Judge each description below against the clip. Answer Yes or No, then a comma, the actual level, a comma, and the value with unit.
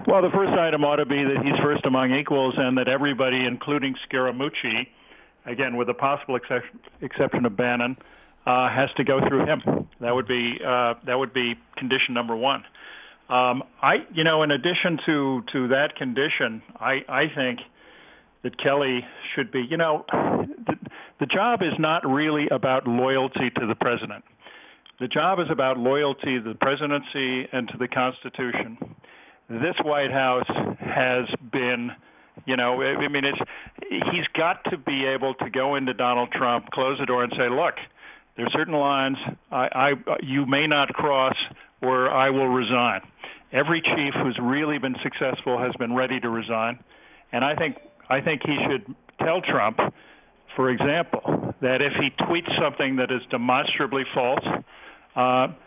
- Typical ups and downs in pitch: No, narrow, 2.0 semitones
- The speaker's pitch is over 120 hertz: Yes, low, 130 Hz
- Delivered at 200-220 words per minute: No, average, 165 wpm